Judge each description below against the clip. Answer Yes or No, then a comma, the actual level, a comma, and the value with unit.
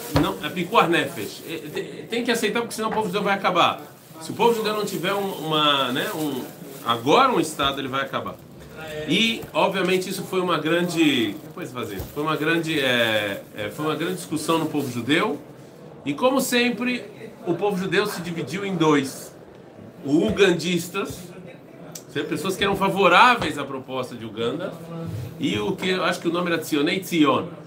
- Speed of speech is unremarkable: Yes, average, 165 wpm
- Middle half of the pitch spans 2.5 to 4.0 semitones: No, average, 4.7 semitones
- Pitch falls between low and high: Yes, medium, 170 Hz